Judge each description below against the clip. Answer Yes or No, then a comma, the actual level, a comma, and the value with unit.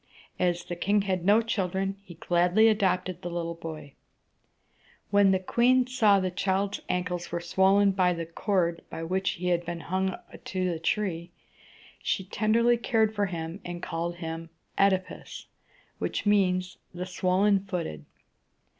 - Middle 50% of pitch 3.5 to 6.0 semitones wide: No, narrow, 2.5 semitones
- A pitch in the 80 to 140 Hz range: No, medium, 185 Hz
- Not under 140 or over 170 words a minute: Yes, average, 155 wpm